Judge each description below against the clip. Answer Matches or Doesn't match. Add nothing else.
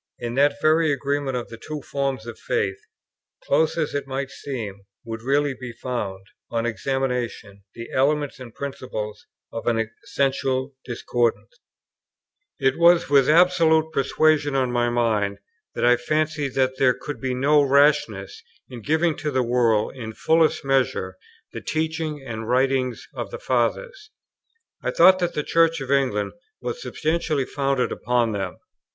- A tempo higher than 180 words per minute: Doesn't match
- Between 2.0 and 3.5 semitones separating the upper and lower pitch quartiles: Doesn't match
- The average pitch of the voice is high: Doesn't match